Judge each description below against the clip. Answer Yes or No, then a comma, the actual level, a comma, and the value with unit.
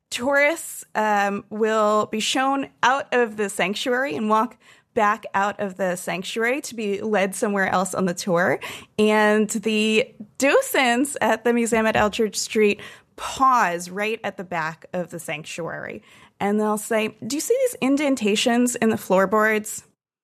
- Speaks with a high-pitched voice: Yes, high, 215 Hz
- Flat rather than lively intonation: No, average, 3.1 semitones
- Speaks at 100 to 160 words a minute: Yes, average, 155 wpm